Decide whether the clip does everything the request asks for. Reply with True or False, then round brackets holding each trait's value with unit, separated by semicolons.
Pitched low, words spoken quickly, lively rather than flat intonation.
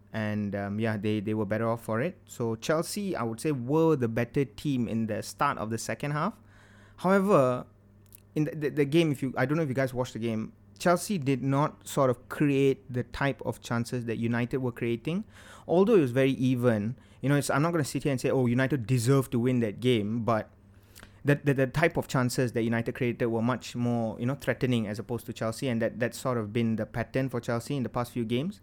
False (120 Hz; 240 wpm; 3.5 semitones)